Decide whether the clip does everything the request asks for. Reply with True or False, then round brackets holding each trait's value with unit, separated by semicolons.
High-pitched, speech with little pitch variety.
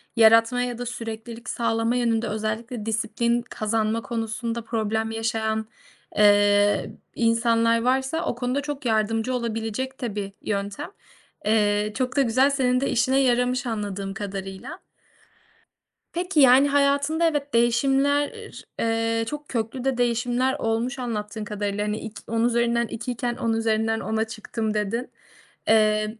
True (230 Hz; 2.3 semitones)